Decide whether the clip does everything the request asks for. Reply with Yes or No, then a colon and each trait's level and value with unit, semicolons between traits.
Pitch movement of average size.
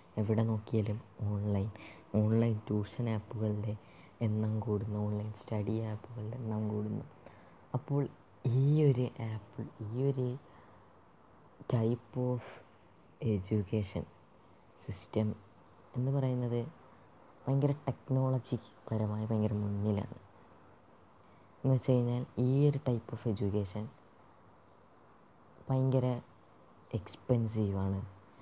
Yes: average, 3.0 semitones